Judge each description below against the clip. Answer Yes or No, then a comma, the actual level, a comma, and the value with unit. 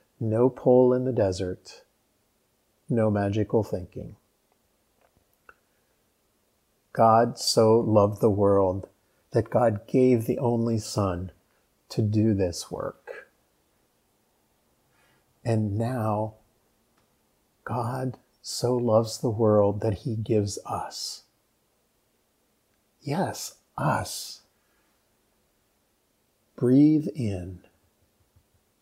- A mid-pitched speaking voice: No, low, 110 Hz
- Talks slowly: Yes, slow, 80 wpm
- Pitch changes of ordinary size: Yes, average, 3.1 semitones